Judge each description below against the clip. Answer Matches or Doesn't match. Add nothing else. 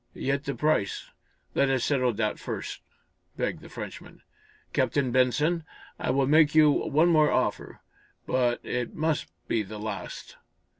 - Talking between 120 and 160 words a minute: Matches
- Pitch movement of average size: Matches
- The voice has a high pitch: Doesn't match